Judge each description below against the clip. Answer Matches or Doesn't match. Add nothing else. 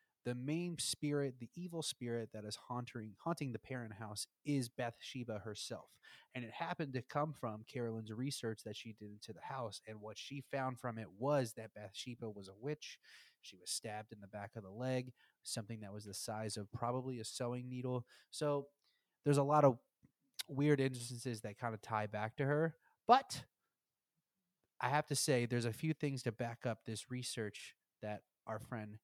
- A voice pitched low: Matches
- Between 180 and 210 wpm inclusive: Matches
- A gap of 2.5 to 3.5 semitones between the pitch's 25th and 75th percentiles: Doesn't match